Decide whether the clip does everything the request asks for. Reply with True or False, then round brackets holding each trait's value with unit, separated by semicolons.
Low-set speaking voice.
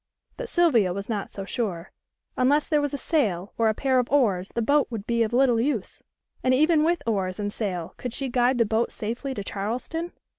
False (235 Hz)